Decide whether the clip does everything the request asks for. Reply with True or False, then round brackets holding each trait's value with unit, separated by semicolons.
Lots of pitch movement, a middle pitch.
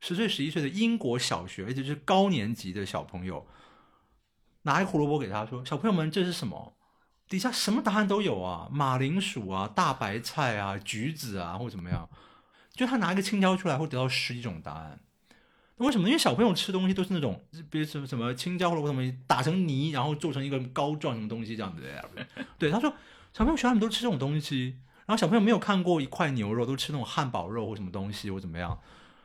True (8.5 semitones; 145 Hz)